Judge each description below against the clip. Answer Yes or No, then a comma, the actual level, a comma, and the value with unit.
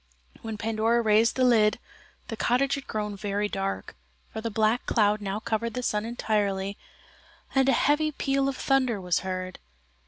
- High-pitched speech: Yes, high, 220 Hz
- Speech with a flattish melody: No, average, 3.2 semitones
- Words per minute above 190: No, average, 165 wpm